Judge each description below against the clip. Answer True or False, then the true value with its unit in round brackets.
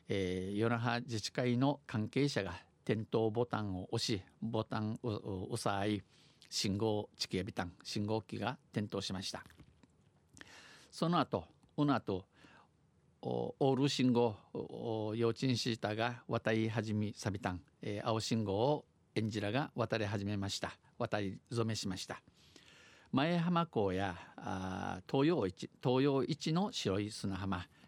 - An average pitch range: True (3.5 semitones)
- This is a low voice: True (110 Hz)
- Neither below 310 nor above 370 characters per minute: False (240 characters per minute)